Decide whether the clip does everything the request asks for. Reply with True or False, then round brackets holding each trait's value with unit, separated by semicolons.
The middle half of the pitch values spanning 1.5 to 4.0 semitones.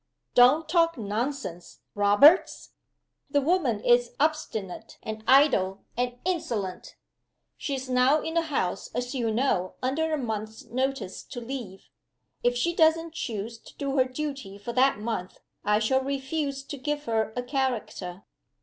False (4.8 semitones)